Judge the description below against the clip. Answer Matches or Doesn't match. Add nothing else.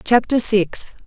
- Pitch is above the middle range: Matches